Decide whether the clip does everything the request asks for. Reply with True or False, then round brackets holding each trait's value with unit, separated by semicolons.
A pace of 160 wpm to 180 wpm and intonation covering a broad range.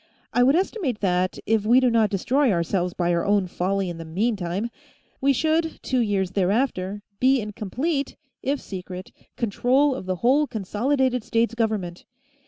True (165 wpm; 5.7 semitones)